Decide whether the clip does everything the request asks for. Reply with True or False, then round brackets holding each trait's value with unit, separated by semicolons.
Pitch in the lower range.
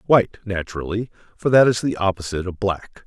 True (100 Hz)